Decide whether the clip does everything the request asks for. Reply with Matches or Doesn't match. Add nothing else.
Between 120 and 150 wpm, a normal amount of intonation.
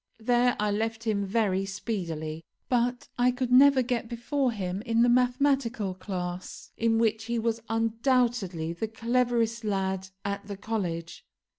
Matches